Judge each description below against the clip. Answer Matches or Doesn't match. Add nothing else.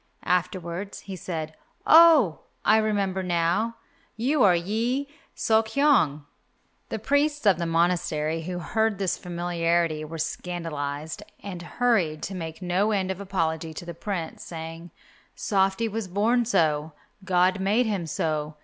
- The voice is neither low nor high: Matches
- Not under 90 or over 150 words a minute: Matches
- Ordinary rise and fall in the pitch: Matches